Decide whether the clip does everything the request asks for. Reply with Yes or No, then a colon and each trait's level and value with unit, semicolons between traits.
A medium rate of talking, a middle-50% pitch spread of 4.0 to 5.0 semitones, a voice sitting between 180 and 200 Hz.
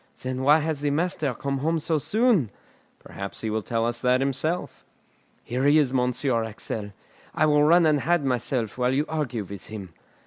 No: average, 185 wpm; average, 4.7 semitones; low, 135 Hz